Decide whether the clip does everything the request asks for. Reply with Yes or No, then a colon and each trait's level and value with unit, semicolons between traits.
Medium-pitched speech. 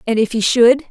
No: high, 235 Hz